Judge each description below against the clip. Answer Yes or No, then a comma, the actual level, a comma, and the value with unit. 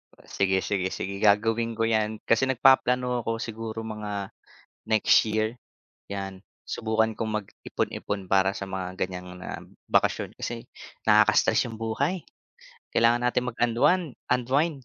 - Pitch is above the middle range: No, low, 110 Hz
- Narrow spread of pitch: No, average, 3.2 semitones